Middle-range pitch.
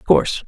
No: very low, 70 Hz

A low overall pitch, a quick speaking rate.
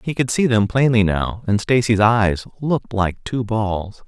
No: low, 110 Hz; average, 190 wpm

